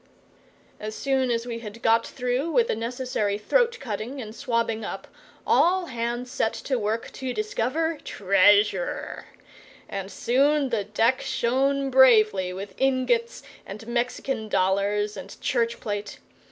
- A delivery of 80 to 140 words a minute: Yes, slow, 135 wpm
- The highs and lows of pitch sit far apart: No, average, 3.8 semitones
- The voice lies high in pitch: Yes, high, 235 Hz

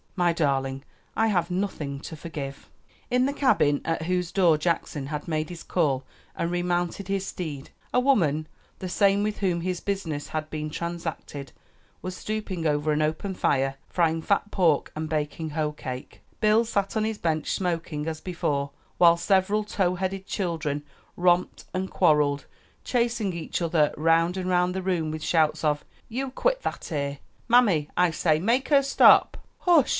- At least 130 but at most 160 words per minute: No, average, 170 wpm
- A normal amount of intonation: Yes, average, 4.1 semitones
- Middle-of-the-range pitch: Yes, medium, 170 Hz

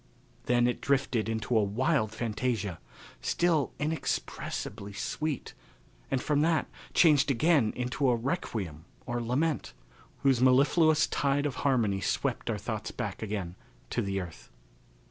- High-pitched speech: No, low, 125 Hz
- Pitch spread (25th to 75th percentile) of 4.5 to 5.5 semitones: Yes, average, 5.1 semitones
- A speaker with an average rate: No, slow, 130 wpm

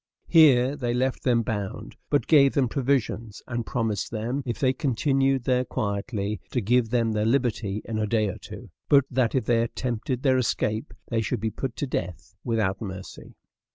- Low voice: Yes, low, 120 Hz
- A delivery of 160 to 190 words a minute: Yes, average, 185 wpm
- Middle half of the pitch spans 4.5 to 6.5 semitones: No, average, 3.3 semitones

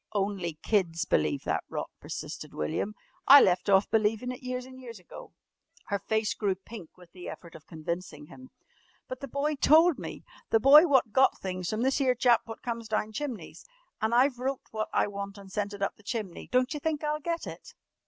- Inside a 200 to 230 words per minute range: Yes, fast, 205 wpm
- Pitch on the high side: Yes, high, 220 Hz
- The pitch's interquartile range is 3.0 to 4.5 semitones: No, average, 5.0 semitones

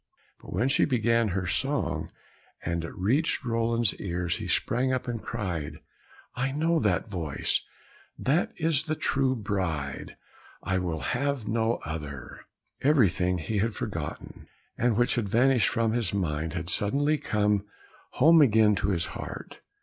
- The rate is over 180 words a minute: No, average, 150 wpm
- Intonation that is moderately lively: No, wide, 6.1 semitones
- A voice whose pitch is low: Yes, low, 110 Hz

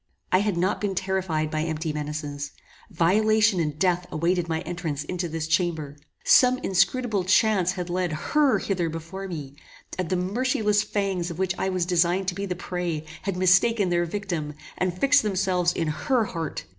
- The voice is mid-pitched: Yes, medium, 180 Hz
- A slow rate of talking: No, average, 180 wpm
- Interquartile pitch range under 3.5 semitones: Yes, average, 3.0 semitones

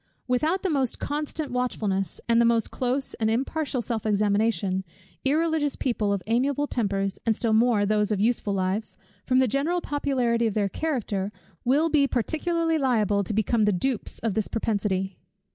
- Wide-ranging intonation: No, average, 4.9 semitones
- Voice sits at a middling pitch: No, high, 235 Hz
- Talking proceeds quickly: No, average, 165 wpm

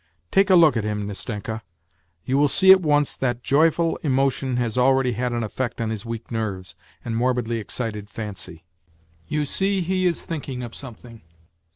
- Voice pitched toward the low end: Yes, low, 125 Hz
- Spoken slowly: No, average, 175 wpm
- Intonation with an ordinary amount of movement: Yes, average, 4.7 semitones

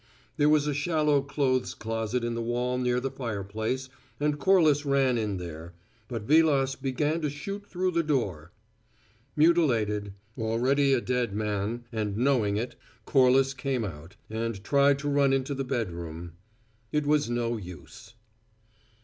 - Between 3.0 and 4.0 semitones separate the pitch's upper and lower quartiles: No, average, 4.6 semitones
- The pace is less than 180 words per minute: Yes, average, 150 wpm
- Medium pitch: No, low, 125 Hz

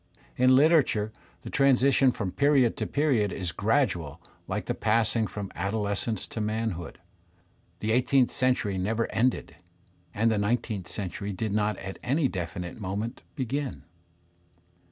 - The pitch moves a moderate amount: Yes, average, 4.3 semitones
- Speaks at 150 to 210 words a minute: No, slow, 135 wpm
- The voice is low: Yes, low, 110 Hz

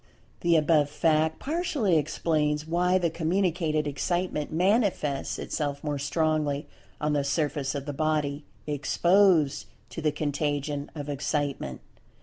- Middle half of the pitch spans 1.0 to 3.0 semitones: Yes, narrow, 2.6 semitones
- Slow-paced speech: Yes, slow, 125 wpm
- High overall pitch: No, medium, 150 Hz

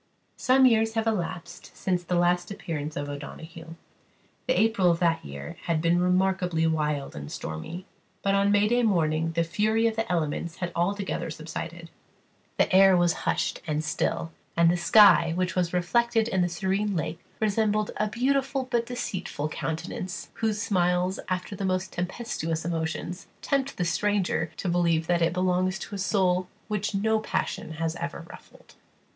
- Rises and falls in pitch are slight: No, average, 3.8 semitones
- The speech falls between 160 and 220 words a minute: Yes, average, 165 wpm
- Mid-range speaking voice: Yes, medium, 180 Hz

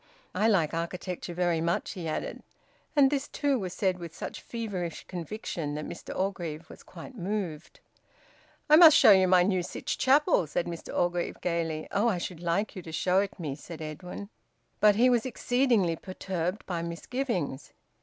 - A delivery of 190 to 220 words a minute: No, average, 175 wpm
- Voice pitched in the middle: Yes, medium, 180 Hz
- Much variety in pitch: No, average, 4.1 semitones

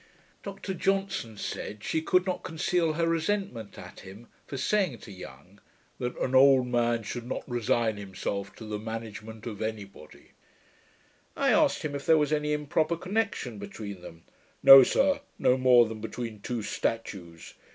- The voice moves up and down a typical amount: No, wide, 6.7 semitones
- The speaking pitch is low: Yes, low, 120 Hz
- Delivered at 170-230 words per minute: No, average, 160 wpm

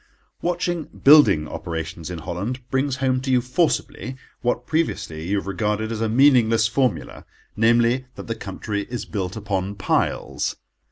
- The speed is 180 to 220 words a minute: No, average, 145 wpm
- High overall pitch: No, low, 115 Hz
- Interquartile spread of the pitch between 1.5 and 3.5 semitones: No, average, 4.8 semitones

